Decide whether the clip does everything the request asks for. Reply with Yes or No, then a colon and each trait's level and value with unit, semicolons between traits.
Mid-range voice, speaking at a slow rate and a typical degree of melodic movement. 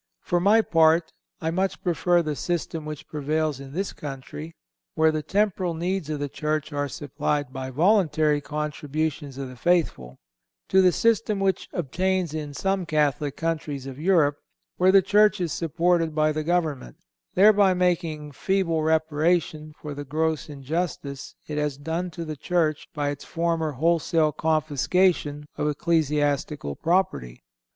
No: medium, 155 Hz; average, 150 wpm; average, 3.1 semitones